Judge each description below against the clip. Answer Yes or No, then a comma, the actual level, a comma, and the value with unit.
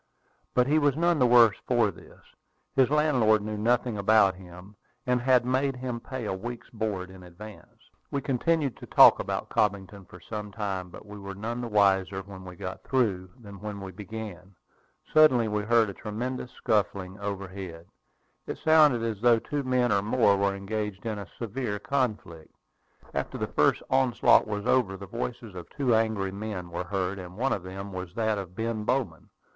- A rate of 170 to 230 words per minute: Yes, average, 185 wpm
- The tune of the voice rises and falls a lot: No, average, 4.0 semitones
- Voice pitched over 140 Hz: No, low, 105 Hz